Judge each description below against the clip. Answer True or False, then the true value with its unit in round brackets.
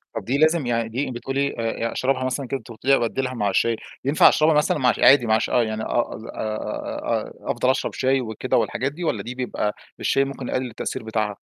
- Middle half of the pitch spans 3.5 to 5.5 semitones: False (3.0 semitones)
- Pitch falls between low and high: False (130 Hz)